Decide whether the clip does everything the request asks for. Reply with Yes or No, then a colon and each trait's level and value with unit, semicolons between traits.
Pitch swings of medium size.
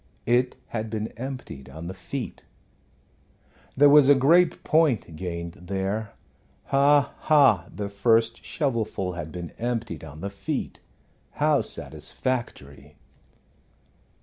No: wide, 6.7 semitones